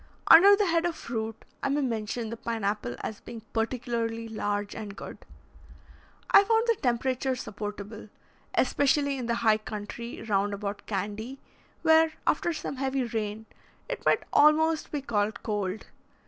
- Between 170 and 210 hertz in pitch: No, high, 230 Hz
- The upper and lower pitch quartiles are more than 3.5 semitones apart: Yes, average, 4.7 semitones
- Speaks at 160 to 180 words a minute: No, average, 150 wpm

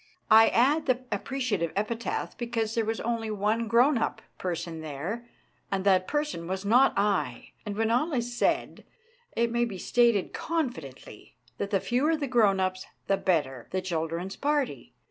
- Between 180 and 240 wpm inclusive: No, average, 165 wpm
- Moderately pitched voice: No, high, 220 Hz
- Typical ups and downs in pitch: Yes, average, 4.5 semitones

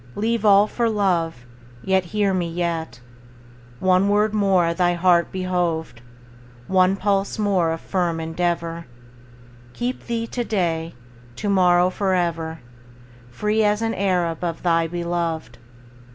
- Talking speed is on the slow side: Yes, slow, 125 wpm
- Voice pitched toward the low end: No, medium, 180 Hz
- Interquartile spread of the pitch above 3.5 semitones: No, average, 3.2 semitones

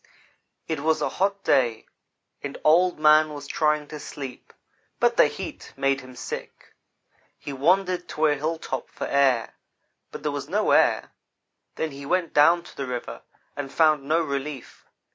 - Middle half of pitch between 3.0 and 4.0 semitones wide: No, narrow, 2.6 semitones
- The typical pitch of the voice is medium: Yes, medium, 150 Hz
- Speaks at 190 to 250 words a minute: No, average, 165 wpm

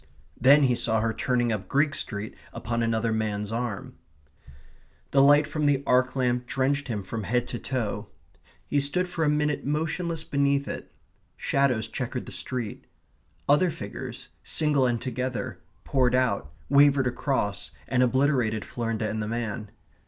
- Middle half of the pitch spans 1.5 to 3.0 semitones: No, average, 3.8 semitones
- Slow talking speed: No, average, 150 wpm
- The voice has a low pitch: Yes, low, 125 Hz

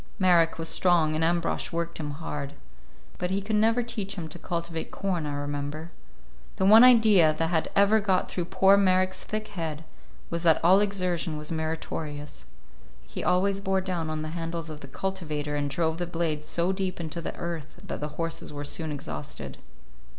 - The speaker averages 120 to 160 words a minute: No, average, 185 wpm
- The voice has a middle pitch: Yes, medium, 170 Hz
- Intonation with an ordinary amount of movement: Yes, average, 3.4 semitones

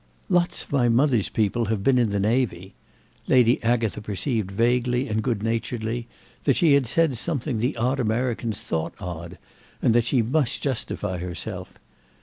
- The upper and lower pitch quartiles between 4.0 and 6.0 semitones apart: No, average, 3.1 semitones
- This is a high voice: No, low, 115 Hz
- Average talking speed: Yes, average, 160 wpm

